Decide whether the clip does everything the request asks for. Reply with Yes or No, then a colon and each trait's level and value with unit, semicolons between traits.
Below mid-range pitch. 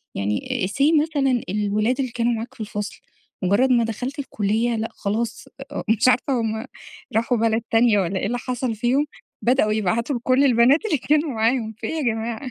No: high, 235 Hz